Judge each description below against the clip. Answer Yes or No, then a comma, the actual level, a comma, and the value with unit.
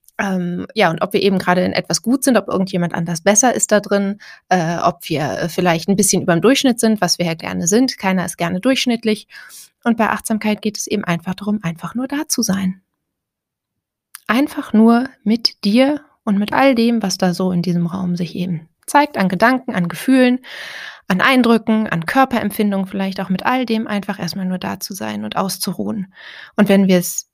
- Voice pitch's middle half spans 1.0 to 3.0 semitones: No, average, 4.1 semitones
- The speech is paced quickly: Yes, fast, 200 wpm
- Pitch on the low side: No, high, 200 Hz